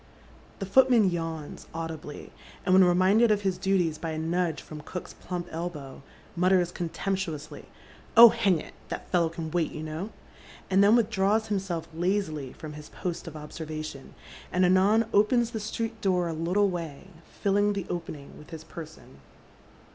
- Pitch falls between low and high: Yes, medium, 180 Hz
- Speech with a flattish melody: No, average, 3.9 semitones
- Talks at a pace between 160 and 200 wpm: Yes, average, 170 wpm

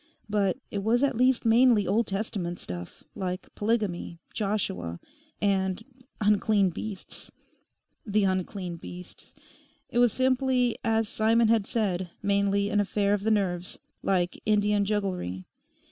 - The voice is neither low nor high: No, high, 205 Hz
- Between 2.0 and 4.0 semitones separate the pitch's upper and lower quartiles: Yes, average, 3.0 semitones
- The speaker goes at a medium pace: No, slow, 130 wpm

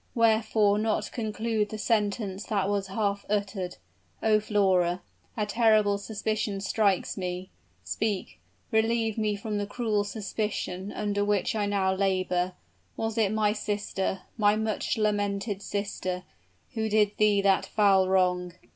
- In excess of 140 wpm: No, slow, 135 wpm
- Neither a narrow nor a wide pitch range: No, narrow, 1.8 semitones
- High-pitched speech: Yes, high, 205 Hz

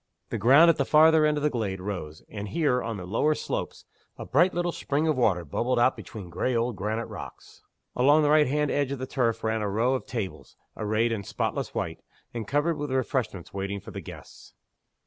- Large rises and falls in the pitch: Yes, wide, 5.8 semitones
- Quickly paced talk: Yes, fast, 215 wpm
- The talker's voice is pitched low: Yes, low, 125 Hz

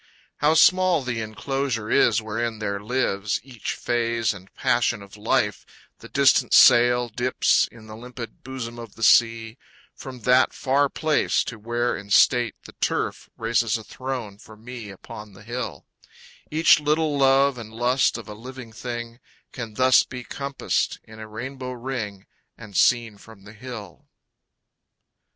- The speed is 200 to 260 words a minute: No, average, 155 wpm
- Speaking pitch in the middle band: No, low, 120 Hz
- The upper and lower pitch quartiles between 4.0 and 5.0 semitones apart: No, average, 2.9 semitones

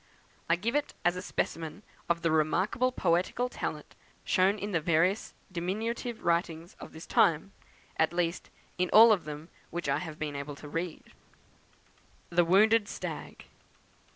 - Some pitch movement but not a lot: Yes, average, 4.0 semitones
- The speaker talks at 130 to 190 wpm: Yes, average, 155 wpm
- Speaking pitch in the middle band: Yes, medium, 175 Hz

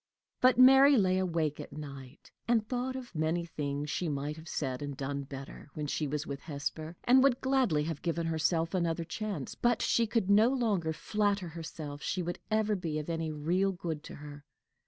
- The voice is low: No, medium, 165 Hz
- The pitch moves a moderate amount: No, wide, 5.9 semitones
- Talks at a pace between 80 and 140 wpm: No, average, 195 wpm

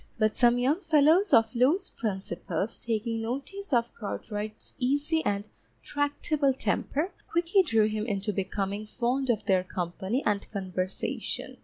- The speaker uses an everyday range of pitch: No, wide, 5.8 semitones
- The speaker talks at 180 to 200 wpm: No, slow, 135 wpm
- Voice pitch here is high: Yes, high, 235 Hz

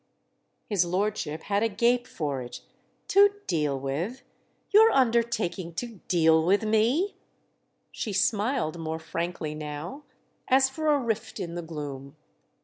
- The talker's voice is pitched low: No, high, 195 Hz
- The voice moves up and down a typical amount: No, wide, 6.8 semitones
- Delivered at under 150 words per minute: Yes, slow, 135 wpm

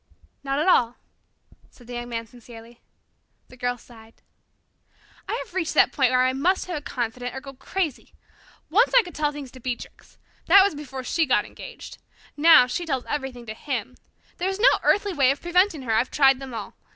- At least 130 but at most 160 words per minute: No, average, 200 wpm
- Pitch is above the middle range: Yes, very high, 265 Hz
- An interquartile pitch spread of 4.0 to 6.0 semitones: Yes, average, 4.8 semitones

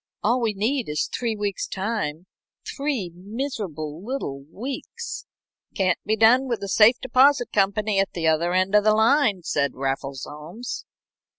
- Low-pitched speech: No, high, 205 Hz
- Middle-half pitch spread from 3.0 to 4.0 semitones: No, wide, 5.6 semitones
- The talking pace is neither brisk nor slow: Yes, average, 155 wpm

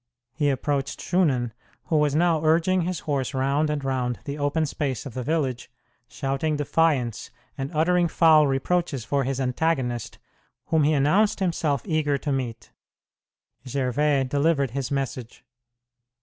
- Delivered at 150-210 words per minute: No, average, 140 wpm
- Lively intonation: No, average, 3.1 semitones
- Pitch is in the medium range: Yes, medium, 145 Hz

